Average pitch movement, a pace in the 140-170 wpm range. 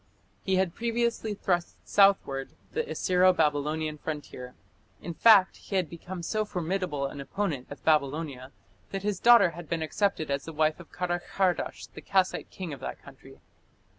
Yes: average, 4.3 semitones; average, 160 wpm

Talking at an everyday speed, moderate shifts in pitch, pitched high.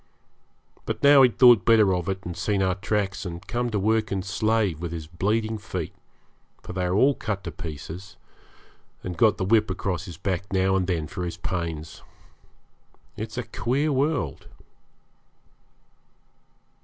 No: average, 165 wpm; average, 3.8 semitones; very low, 95 Hz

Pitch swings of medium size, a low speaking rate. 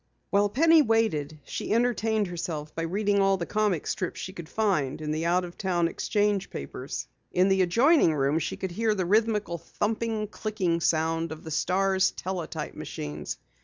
No: average, 4.4 semitones; average, 170 wpm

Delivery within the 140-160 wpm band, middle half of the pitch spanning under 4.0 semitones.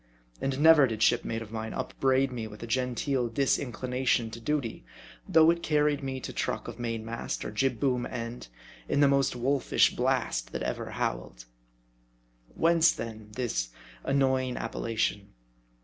Yes: average, 150 wpm; average, 3.3 semitones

